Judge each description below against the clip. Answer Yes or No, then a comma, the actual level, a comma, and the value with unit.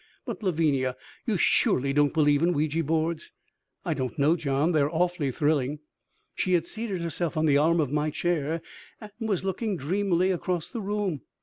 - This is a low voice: No, medium, 160 Hz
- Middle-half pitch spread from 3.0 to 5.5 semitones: Yes, average, 3.4 semitones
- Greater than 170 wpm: Yes, average, 180 wpm